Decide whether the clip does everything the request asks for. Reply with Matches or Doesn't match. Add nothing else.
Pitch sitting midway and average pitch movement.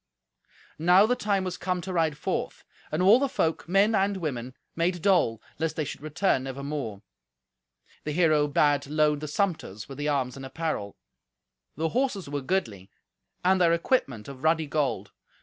Matches